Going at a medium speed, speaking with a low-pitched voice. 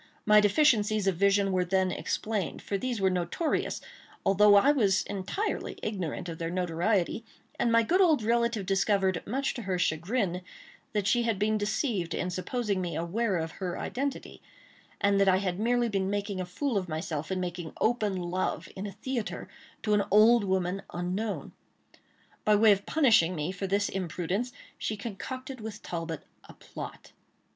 No: average, 170 wpm; high, 200 Hz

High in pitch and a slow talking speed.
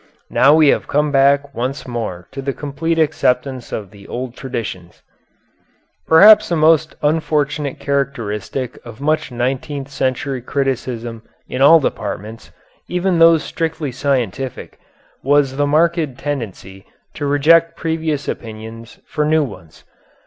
No: medium, 140 Hz; slow, 125 wpm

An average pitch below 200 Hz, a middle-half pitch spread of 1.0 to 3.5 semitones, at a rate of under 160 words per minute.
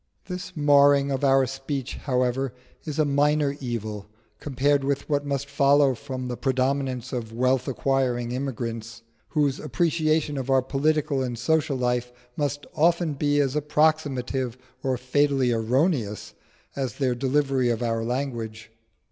Yes: low, 135 Hz; narrow, 2.6 semitones; average, 140 wpm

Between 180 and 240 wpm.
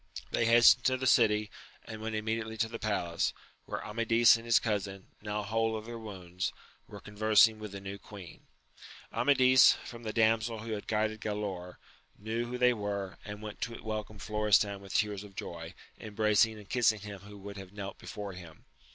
Yes: average, 185 wpm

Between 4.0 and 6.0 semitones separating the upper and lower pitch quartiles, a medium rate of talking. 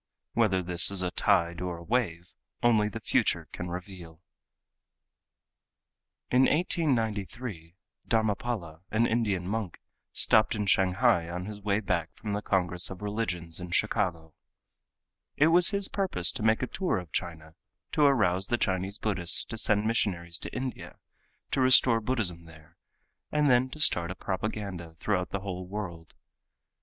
Yes: average, 4.5 semitones; average, 150 wpm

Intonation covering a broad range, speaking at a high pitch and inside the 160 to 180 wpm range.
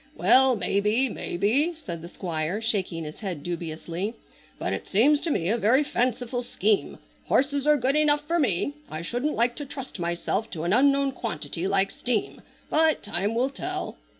Yes: wide, 7.1 semitones; high, 230 Hz; average, 175 wpm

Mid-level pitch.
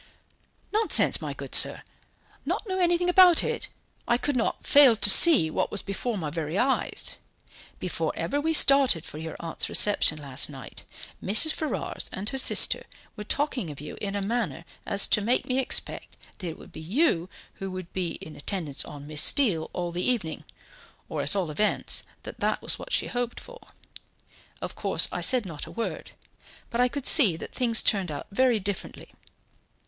No: high, 205 Hz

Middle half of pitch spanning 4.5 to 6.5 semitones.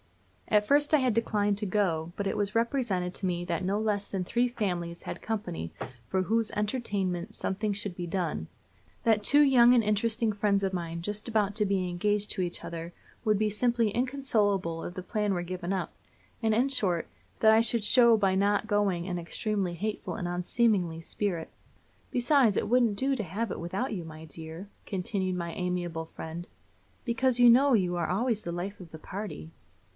No: average, 4.1 semitones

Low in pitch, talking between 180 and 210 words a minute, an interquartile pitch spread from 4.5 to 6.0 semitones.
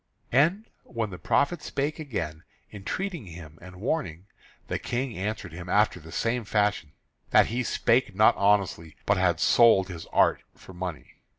No: low, 100 Hz; average, 160 wpm; wide, 5.6 semitones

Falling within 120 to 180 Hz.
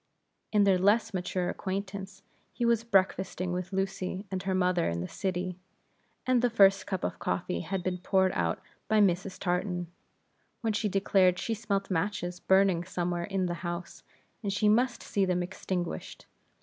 No: high, 190 Hz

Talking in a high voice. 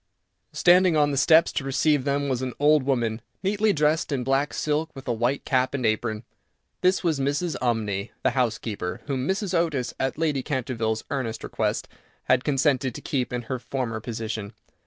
No: low, 135 Hz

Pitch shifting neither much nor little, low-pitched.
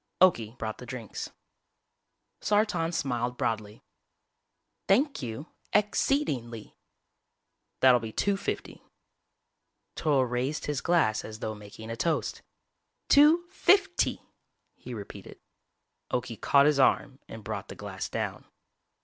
No: wide, 7.6 semitones; low, 130 Hz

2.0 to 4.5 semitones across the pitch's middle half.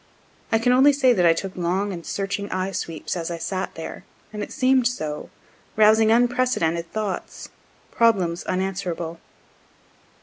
No: average, 5.1 semitones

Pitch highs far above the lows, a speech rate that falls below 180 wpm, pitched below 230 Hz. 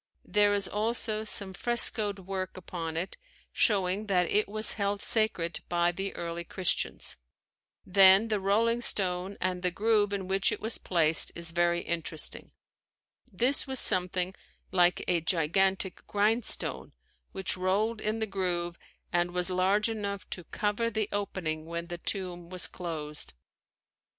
No: average, 3.0 semitones; average, 145 wpm; high, 190 Hz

